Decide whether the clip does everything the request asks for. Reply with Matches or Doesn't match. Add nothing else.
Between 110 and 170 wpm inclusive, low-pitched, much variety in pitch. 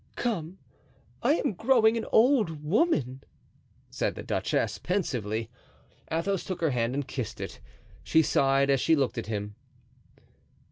Doesn't match